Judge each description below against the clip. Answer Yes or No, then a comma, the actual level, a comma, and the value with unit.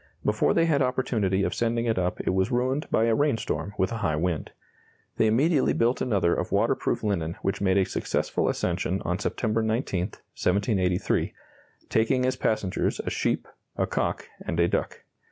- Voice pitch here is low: Yes, low, 110 Hz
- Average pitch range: Yes, average, 4.4 semitones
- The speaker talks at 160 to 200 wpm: Yes, average, 170 wpm